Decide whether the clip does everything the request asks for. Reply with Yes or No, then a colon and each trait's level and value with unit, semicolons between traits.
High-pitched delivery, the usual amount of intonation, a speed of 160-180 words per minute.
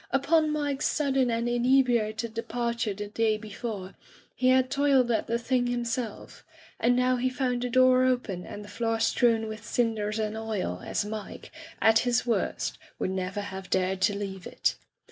Yes: high, 230 Hz; average, 3.1 semitones; average, 170 wpm